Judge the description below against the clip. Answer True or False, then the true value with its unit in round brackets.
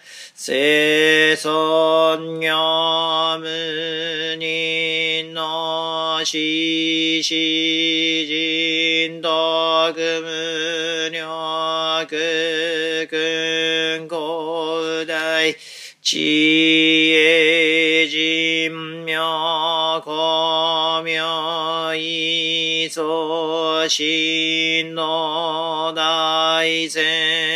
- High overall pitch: False (160 Hz)